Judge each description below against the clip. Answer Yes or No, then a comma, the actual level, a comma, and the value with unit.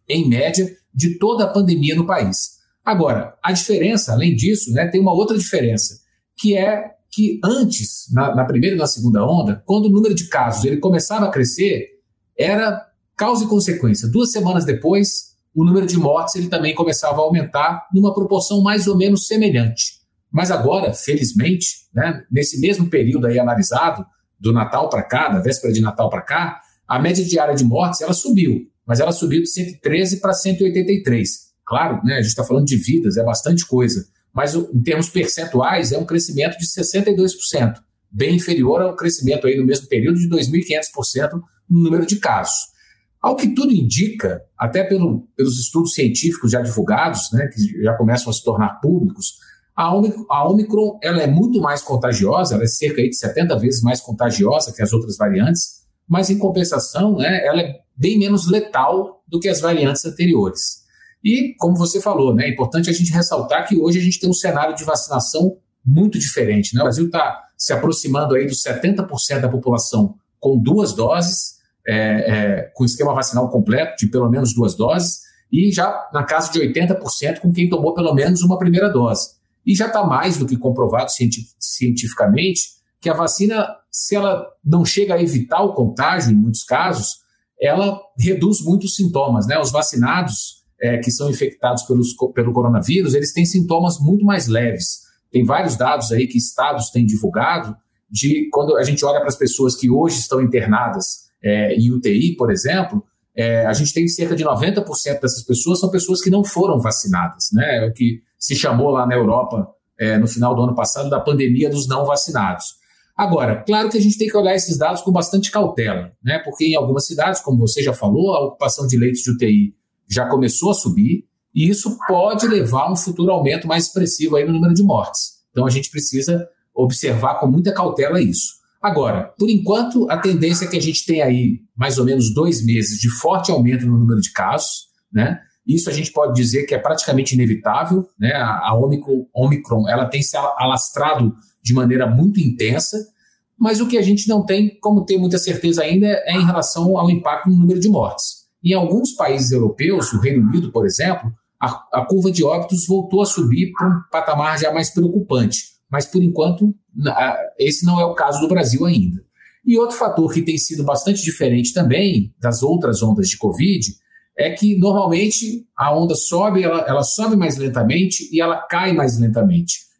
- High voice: No, medium, 160 Hz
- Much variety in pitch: Yes, wide, 7.3 semitones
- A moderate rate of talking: No, fast, 190 wpm